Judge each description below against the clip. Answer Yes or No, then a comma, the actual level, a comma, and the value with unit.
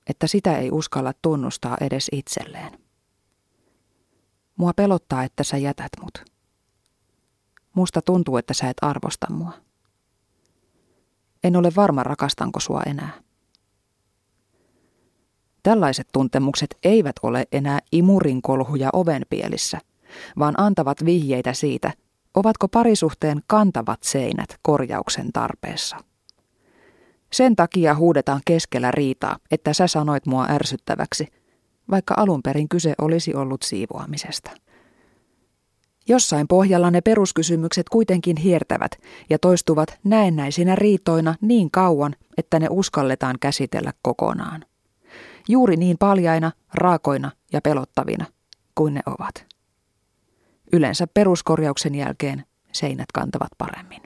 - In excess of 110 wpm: No, average, 100 wpm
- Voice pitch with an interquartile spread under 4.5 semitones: No, average, 4.8 semitones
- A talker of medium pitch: Yes, medium, 155 Hz